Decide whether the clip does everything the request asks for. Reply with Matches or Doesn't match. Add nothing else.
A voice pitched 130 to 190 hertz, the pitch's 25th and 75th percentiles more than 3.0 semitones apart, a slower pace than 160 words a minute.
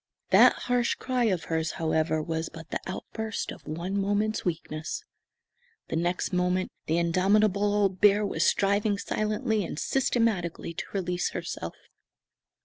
Matches